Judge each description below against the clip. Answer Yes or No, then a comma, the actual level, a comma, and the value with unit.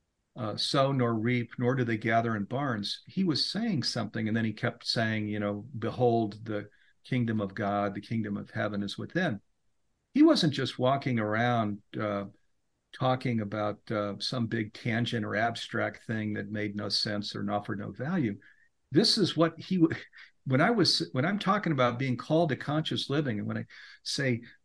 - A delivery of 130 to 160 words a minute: No, average, 185 wpm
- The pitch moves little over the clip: No, average, 4.2 semitones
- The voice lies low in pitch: Yes, low, 115 Hz